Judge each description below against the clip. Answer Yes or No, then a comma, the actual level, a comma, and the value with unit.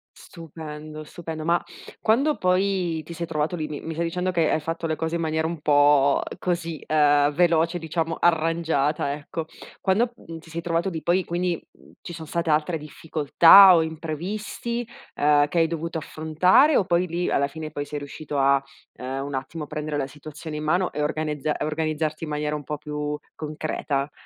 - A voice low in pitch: No, medium, 160 Hz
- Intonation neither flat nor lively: No, narrow, 2.1 semitones